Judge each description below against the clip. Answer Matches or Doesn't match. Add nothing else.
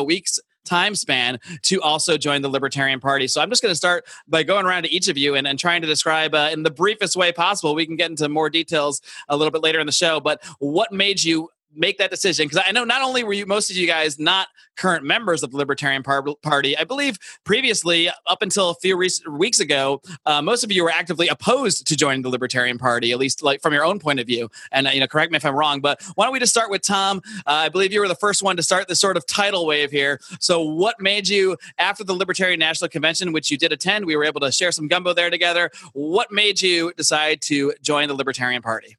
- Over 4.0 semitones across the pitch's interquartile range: Matches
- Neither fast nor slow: Doesn't match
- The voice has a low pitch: Doesn't match